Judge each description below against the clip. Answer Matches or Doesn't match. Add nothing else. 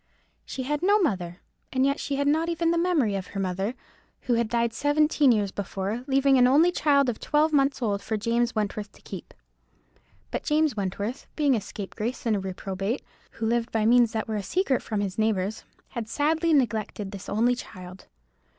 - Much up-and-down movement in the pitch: Matches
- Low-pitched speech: Doesn't match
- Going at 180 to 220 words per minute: Matches